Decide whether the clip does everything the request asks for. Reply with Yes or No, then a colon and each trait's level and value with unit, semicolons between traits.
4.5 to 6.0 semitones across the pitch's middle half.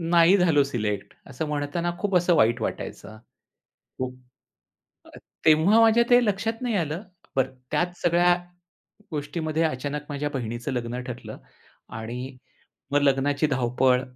Yes: wide, 5.4 semitones